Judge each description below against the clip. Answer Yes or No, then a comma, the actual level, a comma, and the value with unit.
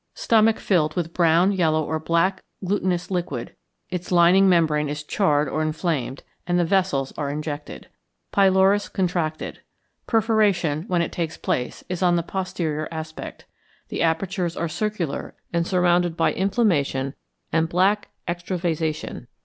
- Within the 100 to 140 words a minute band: Yes, slow, 135 wpm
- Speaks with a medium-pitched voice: Yes, medium, 170 Hz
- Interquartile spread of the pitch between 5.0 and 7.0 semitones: No, average, 3.1 semitones